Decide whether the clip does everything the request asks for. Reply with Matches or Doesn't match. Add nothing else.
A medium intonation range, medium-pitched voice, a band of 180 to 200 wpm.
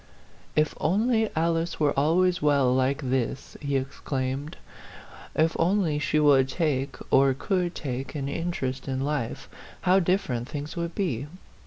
Doesn't match